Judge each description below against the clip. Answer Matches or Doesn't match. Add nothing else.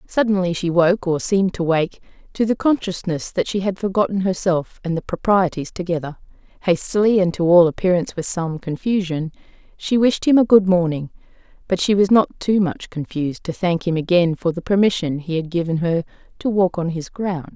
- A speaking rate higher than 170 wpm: Matches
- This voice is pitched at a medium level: Matches